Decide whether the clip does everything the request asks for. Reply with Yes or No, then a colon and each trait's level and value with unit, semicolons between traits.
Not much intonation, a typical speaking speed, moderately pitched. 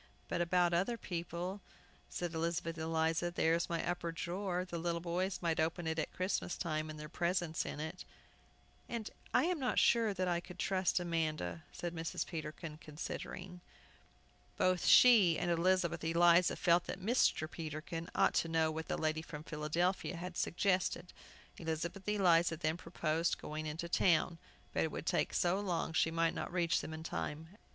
Yes: narrow, 1.9 semitones; average, 170 wpm; medium, 170 Hz